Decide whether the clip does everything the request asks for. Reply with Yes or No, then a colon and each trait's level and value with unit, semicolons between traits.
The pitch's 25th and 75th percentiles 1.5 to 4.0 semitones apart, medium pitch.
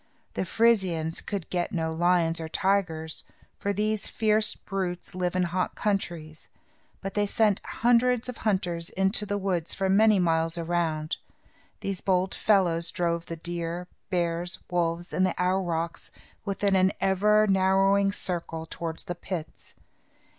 Yes: average, 2.9 semitones; medium, 180 Hz